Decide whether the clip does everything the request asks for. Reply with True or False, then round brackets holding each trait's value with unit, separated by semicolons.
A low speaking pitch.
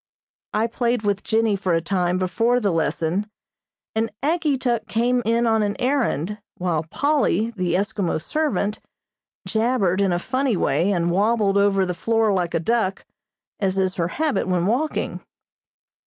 False (205 Hz)